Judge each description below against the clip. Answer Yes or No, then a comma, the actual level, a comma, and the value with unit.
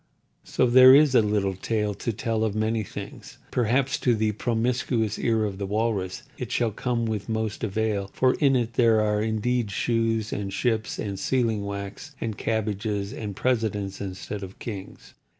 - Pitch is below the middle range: Yes, low, 110 Hz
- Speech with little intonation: Yes, narrow, 2.3 semitones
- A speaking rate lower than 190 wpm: Yes, average, 175 wpm